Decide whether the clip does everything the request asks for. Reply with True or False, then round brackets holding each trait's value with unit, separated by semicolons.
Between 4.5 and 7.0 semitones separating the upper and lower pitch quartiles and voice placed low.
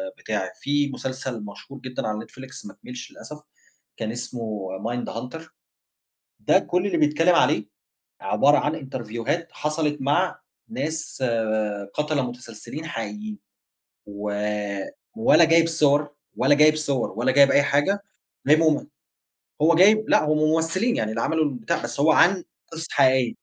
False (4.8 semitones; 145 Hz)